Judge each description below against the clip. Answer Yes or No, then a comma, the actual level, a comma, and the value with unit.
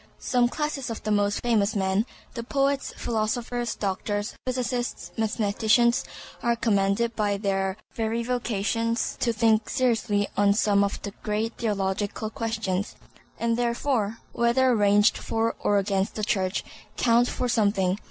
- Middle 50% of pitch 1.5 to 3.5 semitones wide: Yes, average, 2.7 semitones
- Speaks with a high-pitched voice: Yes, high, 220 Hz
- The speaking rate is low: Yes, slow, 130 wpm